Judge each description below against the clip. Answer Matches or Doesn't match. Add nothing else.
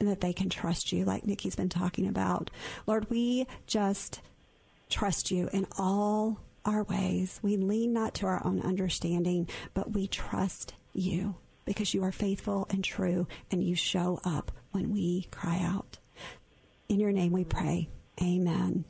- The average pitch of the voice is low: Doesn't match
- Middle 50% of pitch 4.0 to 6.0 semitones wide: Doesn't match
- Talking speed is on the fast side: Doesn't match